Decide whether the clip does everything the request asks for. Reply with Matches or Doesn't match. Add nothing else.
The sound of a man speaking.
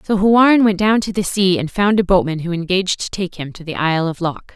Doesn't match